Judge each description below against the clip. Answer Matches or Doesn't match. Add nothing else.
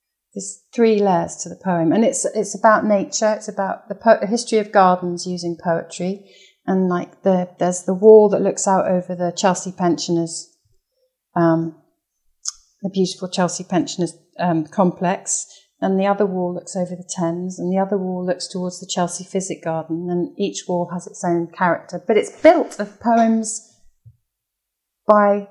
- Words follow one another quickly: Doesn't match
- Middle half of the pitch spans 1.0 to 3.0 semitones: Matches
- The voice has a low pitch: Doesn't match